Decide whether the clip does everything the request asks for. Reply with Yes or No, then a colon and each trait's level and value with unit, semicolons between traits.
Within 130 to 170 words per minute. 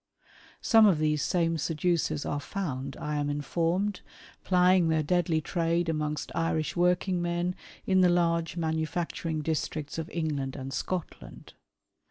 Yes: slow, 135 wpm